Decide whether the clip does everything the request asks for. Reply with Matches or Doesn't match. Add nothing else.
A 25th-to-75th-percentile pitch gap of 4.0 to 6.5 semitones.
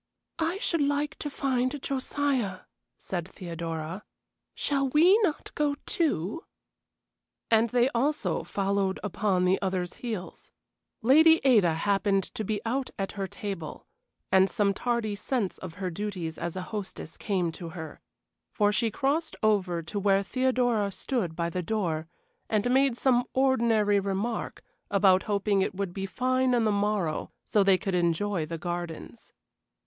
Matches